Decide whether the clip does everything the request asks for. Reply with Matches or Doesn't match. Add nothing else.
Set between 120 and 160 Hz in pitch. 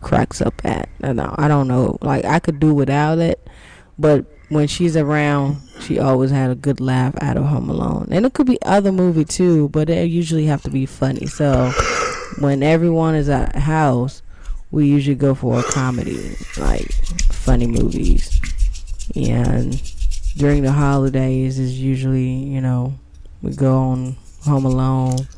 Matches